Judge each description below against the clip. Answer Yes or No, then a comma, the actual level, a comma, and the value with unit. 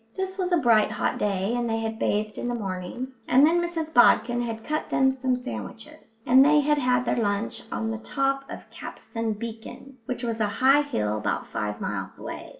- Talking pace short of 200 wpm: No, fast, 205 wpm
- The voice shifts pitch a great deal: No, average, 3.6 semitones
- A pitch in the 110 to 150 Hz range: No, high, 240 Hz